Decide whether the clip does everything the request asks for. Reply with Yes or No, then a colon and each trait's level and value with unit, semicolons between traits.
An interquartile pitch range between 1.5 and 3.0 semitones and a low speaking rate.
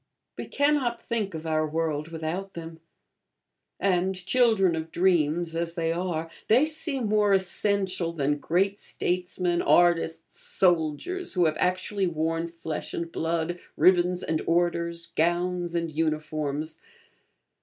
Yes: average, 2.7 semitones; slow, 125 wpm